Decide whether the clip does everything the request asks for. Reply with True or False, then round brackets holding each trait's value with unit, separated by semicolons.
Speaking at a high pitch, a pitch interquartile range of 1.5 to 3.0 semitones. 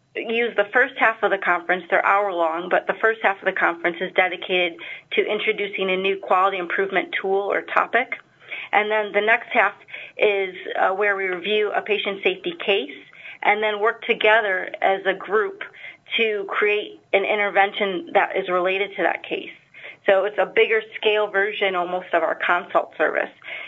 True (200 Hz; 2.7 semitones)